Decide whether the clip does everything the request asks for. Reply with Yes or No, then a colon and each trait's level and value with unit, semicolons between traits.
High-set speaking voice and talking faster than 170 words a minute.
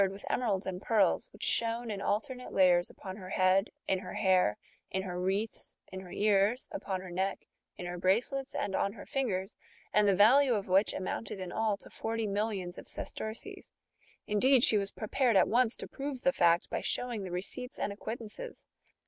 Yes: high, 205 Hz; average, 195 wpm